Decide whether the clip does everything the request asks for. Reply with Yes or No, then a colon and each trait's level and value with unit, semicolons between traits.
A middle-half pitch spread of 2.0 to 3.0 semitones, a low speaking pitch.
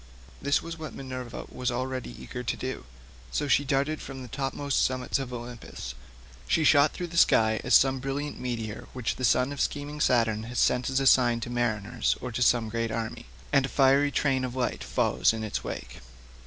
Yes: narrow, 2.6 semitones; low, 130 Hz